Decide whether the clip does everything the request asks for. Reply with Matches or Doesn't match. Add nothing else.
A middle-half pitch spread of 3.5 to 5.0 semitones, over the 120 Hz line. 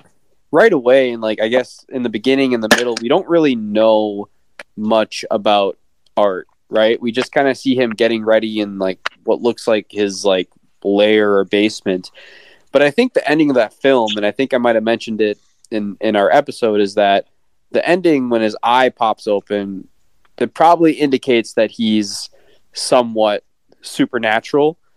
Doesn't match